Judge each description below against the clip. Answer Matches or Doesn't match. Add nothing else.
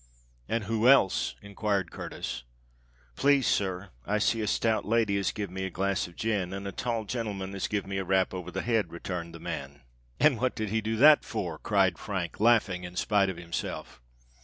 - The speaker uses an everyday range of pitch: Matches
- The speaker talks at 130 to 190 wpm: Doesn't match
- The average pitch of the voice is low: Matches